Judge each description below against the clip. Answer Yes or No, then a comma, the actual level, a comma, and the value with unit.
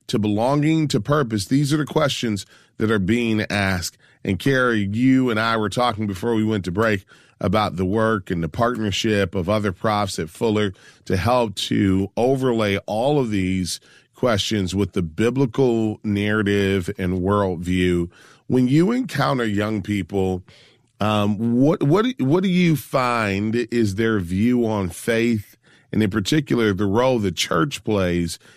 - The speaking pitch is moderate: No, low, 110 Hz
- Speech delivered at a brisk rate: No, average, 155 wpm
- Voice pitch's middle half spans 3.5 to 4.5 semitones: Yes, average, 3.8 semitones